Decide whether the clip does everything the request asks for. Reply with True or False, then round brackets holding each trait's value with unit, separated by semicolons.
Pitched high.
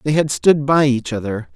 False (135 Hz)